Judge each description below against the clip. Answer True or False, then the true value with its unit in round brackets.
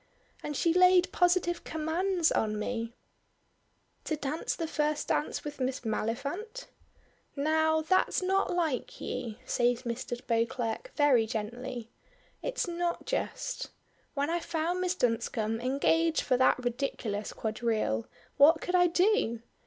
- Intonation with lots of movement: True (6.6 semitones)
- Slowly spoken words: True (130 wpm)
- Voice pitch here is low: False (290 Hz)